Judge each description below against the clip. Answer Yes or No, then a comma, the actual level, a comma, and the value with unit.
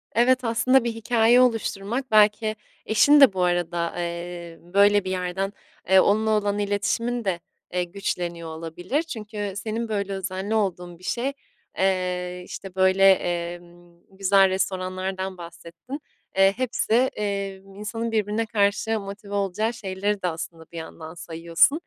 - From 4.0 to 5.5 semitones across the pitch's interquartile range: No, average, 3.5 semitones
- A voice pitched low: No, high, 195 Hz